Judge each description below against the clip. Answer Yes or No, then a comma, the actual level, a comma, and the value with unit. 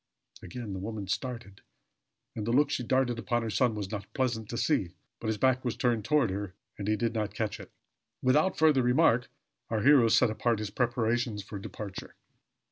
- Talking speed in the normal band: Yes, average, 195 wpm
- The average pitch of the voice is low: Yes, low, 115 Hz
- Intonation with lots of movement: No, average, 3.2 semitones